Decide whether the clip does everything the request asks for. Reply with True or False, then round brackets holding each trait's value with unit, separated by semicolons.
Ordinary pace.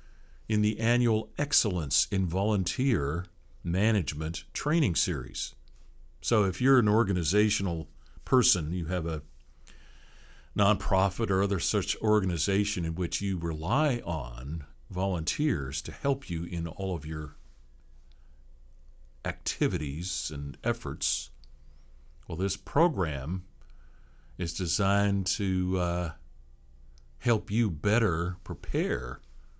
False (100 wpm)